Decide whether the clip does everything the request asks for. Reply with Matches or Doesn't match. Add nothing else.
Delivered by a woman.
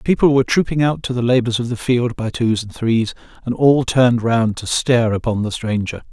Doesn't match